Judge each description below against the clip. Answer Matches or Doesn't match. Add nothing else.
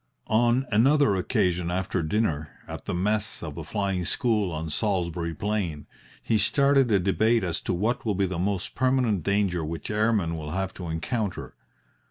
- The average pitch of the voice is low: Matches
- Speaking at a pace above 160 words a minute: Matches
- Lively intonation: Doesn't match